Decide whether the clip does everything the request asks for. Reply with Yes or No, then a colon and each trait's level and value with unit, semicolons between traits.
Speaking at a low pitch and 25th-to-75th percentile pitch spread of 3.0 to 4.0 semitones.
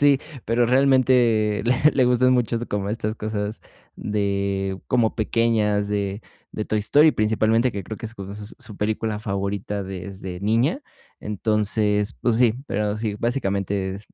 No: low, 105 Hz; narrow, 2.5 semitones